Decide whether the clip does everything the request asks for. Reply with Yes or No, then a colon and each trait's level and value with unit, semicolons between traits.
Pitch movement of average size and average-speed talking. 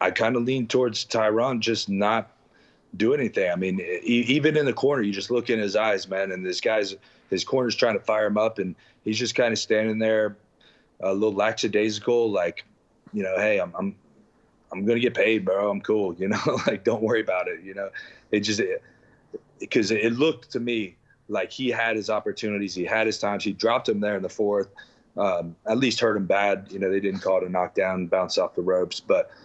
No: average, 3.1 semitones; fast, 220 wpm